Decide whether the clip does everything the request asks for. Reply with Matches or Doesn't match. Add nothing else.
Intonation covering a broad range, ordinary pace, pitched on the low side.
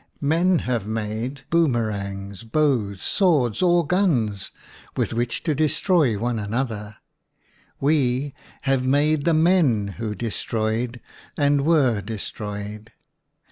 Doesn't match